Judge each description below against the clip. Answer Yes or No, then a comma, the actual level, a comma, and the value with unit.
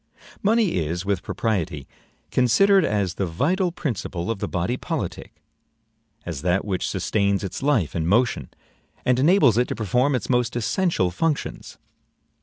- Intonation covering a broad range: Yes, wide, 7.5 semitones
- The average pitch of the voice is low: Yes, low, 115 Hz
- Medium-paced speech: Yes, average, 145 wpm